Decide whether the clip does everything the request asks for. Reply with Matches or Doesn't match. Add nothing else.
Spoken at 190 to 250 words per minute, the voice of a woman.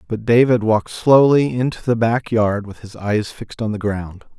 Doesn't match